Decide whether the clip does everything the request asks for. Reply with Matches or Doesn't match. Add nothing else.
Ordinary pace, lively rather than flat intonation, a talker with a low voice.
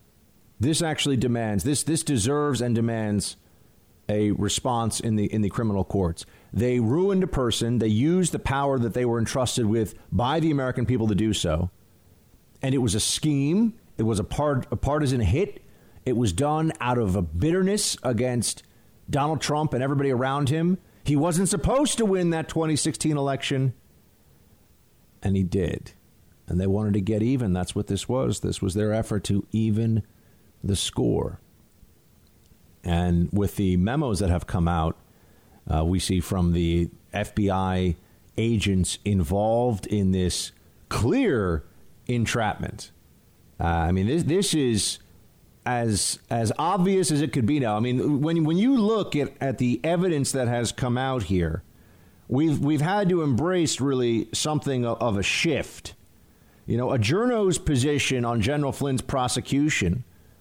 Matches